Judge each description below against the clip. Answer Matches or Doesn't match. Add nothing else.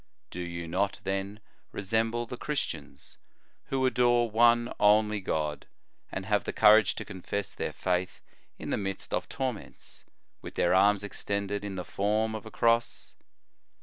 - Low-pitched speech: Matches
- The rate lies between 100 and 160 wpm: Matches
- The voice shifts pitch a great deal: Doesn't match